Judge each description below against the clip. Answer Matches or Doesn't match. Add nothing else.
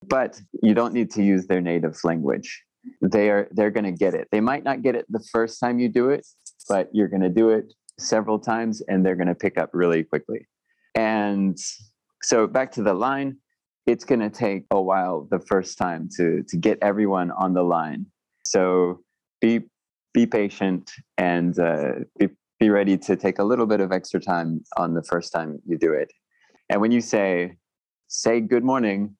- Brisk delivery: Doesn't match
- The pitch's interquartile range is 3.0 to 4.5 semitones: Matches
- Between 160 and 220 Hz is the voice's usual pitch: Doesn't match